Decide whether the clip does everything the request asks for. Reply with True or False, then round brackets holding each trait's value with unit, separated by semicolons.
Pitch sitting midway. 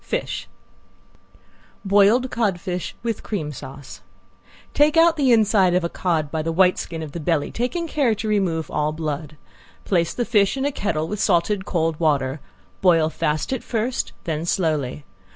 True (180 Hz)